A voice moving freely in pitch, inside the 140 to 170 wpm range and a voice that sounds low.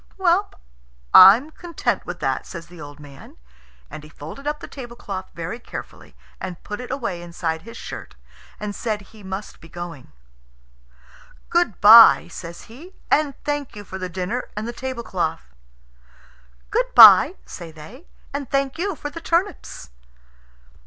No: wide, 8.2 semitones; average, 150 wpm; high, 210 Hz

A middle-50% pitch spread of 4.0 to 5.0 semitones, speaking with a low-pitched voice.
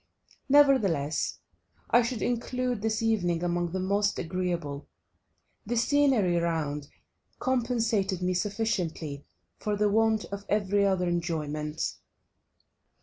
No: average, 4.7 semitones; high, 195 Hz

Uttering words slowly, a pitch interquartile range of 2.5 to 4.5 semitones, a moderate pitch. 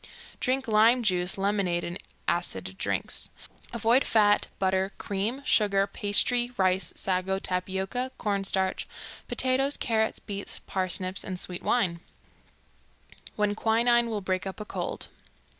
No: slow, 125 wpm; average, 3.6 semitones; high, 200 Hz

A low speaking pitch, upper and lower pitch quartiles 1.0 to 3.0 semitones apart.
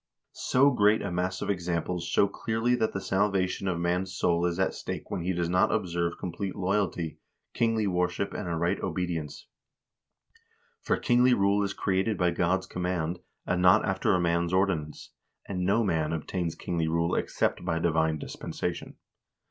Yes: very low, 90 Hz; narrow, 2.5 semitones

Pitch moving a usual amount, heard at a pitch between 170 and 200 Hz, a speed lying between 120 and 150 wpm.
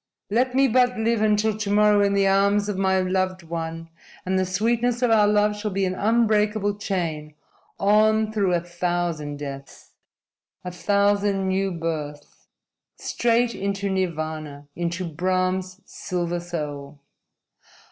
Yes: average, 3.4 semitones; high, 190 Hz; slow, 135 wpm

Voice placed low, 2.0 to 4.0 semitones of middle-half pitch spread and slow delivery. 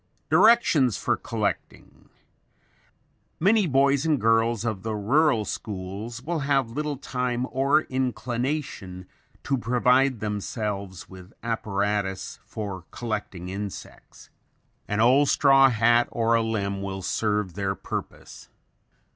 No: low, 115 Hz; average, 4.9 semitones; slow, 115 wpm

